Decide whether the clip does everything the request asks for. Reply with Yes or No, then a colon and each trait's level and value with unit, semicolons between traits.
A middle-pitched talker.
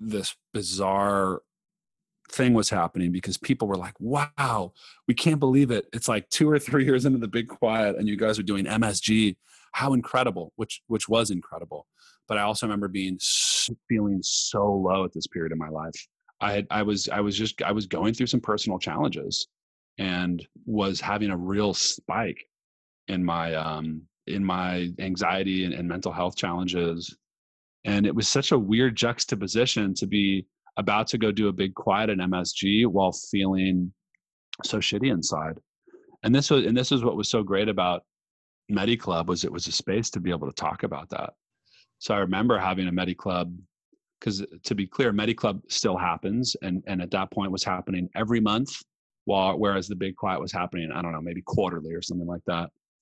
No: low, 100 Hz